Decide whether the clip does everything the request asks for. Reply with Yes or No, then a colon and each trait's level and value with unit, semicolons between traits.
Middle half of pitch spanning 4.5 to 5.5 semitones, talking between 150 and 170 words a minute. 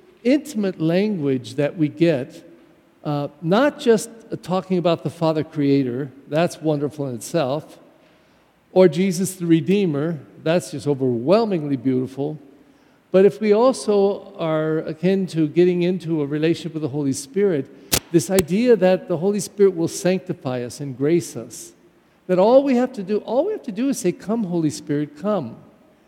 Yes: average, 4.9 semitones; average, 160 wpm